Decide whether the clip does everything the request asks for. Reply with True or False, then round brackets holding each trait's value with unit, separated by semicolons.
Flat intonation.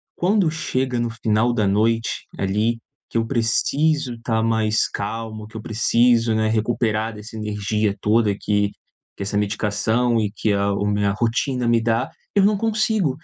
True (2.3 semitones)